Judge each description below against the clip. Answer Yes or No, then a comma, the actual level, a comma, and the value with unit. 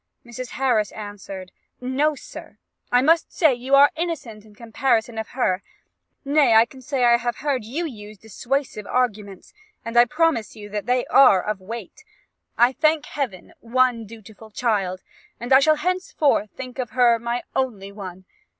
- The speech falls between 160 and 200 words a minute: Yes, average, 165 wpm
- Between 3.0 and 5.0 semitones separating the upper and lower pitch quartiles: Yes, average, 4.1 semitones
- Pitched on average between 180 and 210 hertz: No, high, 240 Hz